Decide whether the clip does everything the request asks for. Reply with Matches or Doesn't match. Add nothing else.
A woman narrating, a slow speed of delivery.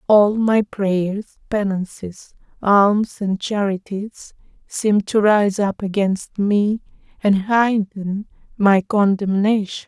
Matches